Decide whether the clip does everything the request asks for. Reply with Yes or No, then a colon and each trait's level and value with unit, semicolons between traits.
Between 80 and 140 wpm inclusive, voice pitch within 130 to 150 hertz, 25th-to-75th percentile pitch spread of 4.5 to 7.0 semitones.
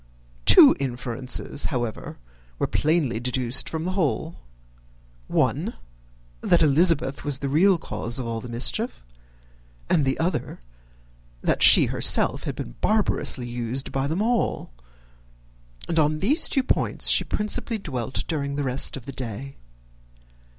Yes: slow, 135 wpm; medium, 140 Hz; average, 5.0 semitones